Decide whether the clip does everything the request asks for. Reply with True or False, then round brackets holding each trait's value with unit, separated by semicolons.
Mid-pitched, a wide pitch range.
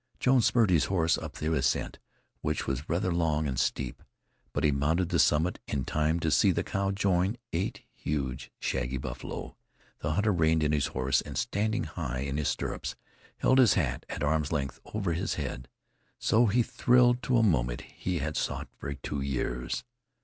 False (80 Hz; 5.8 semitones)